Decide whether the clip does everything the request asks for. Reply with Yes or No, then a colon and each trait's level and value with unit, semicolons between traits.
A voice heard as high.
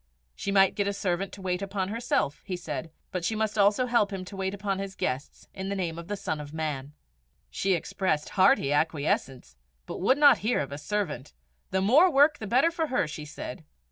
Yes: high, 195 Hz